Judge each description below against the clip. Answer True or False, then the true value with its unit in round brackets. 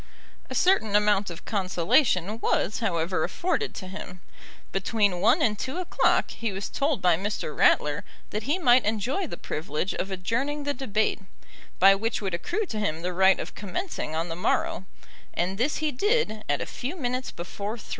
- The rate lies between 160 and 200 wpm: True (180 wpm)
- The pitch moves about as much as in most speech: False (5.9 semitones)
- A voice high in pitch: True (210 Hz)